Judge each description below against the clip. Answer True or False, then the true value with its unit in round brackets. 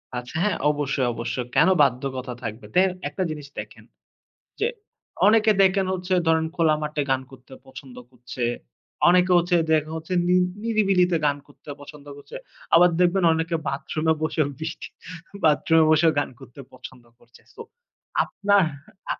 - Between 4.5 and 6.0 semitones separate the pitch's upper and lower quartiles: True (4.9 semitones)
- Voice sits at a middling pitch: True (155 Hz)